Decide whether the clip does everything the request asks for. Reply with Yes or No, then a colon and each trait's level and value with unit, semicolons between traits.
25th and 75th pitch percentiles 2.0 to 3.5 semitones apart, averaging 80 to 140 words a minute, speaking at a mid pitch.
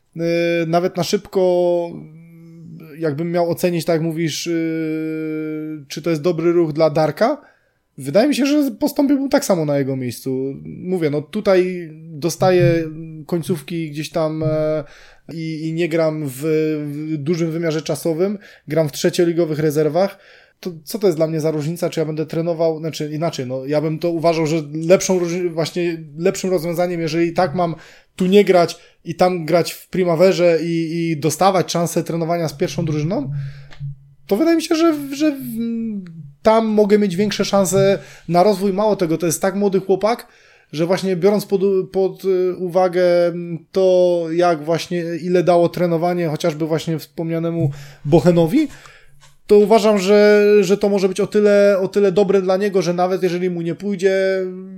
No: average, 3.0 semitones; fast, 160 wpm; medium, 170 Hz